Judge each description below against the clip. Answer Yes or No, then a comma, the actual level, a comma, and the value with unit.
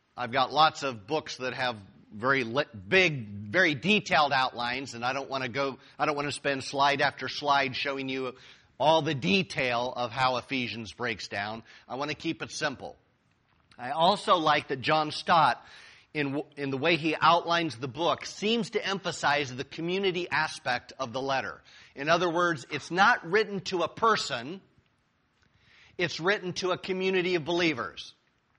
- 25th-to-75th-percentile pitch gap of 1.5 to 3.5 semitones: No, average, 4.7 semitones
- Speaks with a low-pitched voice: No, medium, 145 Hz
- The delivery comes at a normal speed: Yes, average, 160 wpm